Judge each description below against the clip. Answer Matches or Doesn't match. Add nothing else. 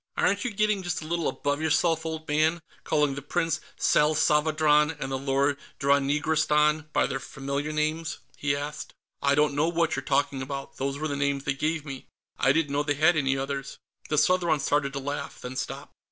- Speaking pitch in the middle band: Matches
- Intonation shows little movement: Matches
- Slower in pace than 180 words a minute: Doesn't match